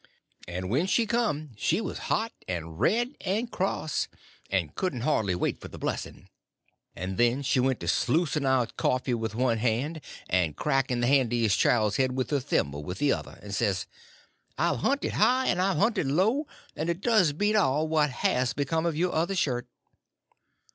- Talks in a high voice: No, low, 135 Hz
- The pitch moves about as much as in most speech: No, wide, 7.4 semitones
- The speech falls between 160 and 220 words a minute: Yes, average, 180 wpm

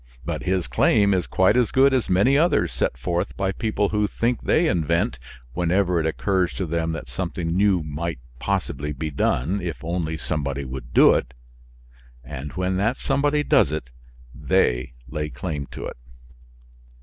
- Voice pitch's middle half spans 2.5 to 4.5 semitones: No, average, 4.9 semitones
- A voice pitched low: Yes, very low, 85 Hz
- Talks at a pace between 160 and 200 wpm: Yes, average, 170 wpm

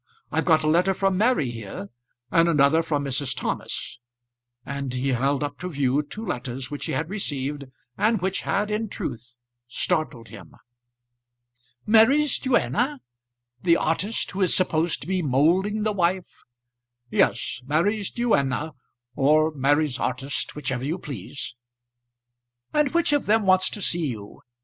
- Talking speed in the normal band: Yes, average, 145 wpm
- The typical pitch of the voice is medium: Yes, medium, 160 Hz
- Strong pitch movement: Yes, wide, 6.1 semitones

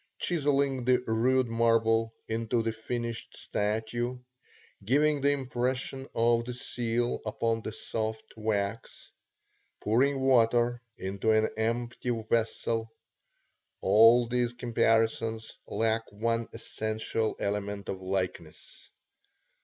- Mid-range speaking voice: No, low, 115 Hz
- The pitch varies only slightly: Yes, narrow, 1.7 semitones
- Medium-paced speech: No, slow, 100 wpm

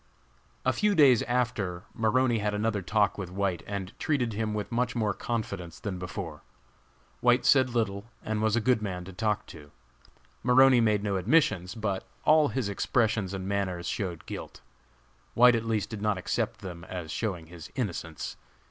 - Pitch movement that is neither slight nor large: Yes, average, 4.0 semitones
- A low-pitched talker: Yes, low, 105 Hz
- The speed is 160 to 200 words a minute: Yes, average, 170 wpm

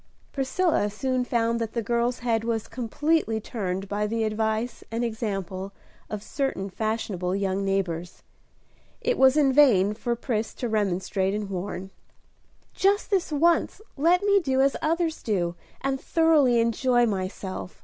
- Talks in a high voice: Yes, high, 230 Hz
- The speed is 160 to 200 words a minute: No, average, 145 wpm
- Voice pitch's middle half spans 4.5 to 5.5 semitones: Yes, average, 5.2 semitones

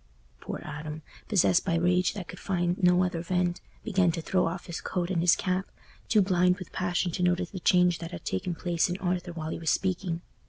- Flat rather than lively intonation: Yes, narrow, 1.3 semitones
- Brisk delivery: Yes, fast, 220 wpm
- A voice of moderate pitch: Yes, medium, 180 Hz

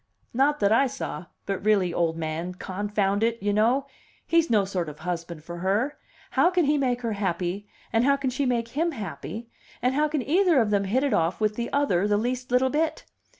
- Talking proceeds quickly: Yes, fast, 215 wpm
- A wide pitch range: Yes, wide, 6.1 semitones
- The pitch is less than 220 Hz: No, high, 225 Hz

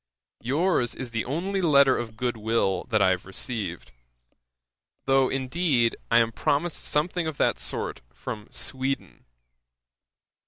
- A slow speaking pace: Yes, slow, 125 wpm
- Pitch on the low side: Yes, low, 130 Hz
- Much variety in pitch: No, average, 4.6 semitones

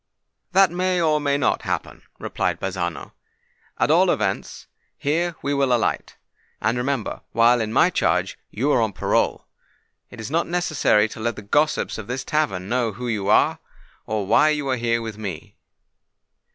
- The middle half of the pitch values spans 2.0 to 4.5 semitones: No, wide, 5.4 semitones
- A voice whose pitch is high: No, low, 125 Hz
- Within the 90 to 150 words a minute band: No, average, 175 wpm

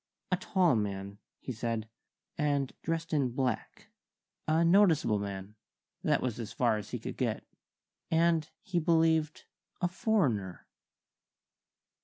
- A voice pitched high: No, medium, 145 Hz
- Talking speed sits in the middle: No, slow, 125 wpm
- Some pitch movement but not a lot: No, wide, 7.1 semitones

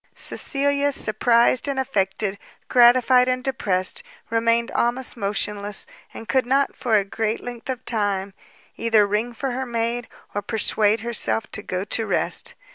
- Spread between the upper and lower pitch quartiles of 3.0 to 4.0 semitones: Yes, average, 3.3 semitones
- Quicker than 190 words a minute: No, average, 145 wpm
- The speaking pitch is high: Yes, high, 230 Hz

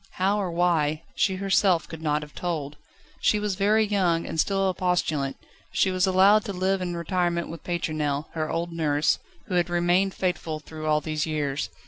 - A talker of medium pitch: Yes, medium, 175 Hz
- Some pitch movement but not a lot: Yes, average, 3.3 semitones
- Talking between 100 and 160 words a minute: No, average, 185 wpm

